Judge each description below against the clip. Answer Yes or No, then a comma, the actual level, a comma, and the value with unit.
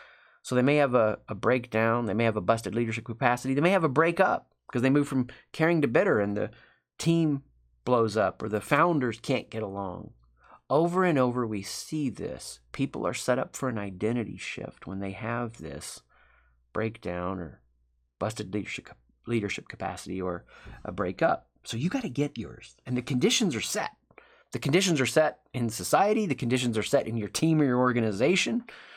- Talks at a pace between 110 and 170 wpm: No, average, 190 wpm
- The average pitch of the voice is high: No, low, 120 Hz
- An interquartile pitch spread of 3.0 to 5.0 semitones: No, wide, 5.5 semitones